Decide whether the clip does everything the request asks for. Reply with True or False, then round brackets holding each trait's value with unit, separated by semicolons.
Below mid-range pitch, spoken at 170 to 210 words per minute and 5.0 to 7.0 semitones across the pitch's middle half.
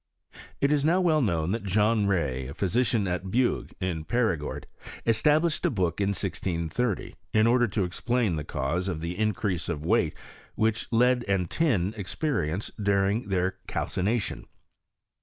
False (100 Hz; 150 wpm; 5.3 semitones)